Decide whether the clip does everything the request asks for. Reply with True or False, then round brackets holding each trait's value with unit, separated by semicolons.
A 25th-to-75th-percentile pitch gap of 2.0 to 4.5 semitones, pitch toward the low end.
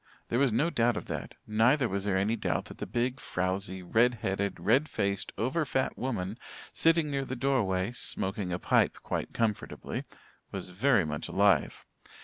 False (5.2 semitones; 110 Hz)